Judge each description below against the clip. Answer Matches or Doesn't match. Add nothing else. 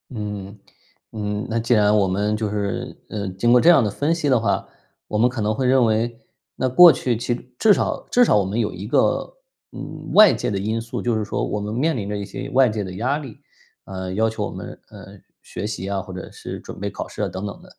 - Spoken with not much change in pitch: Doesn't match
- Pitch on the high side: Doesn't match